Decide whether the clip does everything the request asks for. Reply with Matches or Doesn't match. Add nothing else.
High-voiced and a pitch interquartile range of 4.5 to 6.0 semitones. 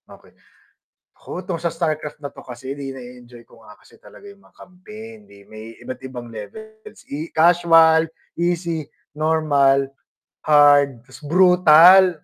Doesn't match